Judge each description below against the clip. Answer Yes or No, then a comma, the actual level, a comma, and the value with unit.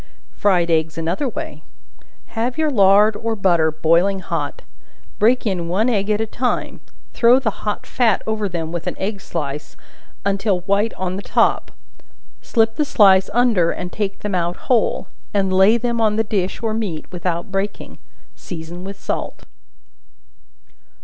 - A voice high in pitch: Yes, high, 200 Hz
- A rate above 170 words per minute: No, average, 155 wpm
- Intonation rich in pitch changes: No, average, 4.0 semitones